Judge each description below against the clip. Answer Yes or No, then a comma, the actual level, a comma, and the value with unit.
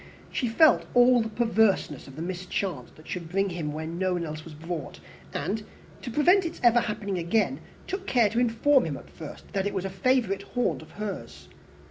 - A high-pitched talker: Yes, high, 195 Hz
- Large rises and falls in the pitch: Yes, wide, 6.1 semitones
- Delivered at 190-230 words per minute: Yes, average, 200 wpm